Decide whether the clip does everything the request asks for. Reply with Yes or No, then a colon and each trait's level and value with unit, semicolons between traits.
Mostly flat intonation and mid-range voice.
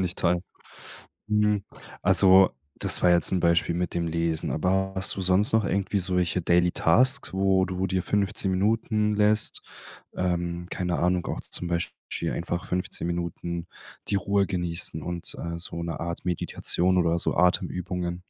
No: narrow, 1.9 semitones; very low, 90 Hz